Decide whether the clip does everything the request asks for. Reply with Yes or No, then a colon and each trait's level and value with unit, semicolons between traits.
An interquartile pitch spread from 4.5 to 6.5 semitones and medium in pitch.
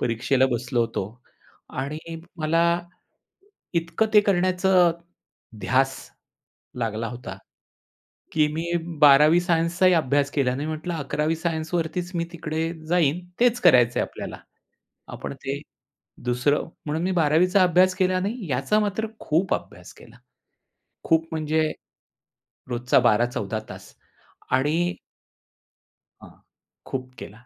Yes: average, 5.0 semitones; medium, 160 Hz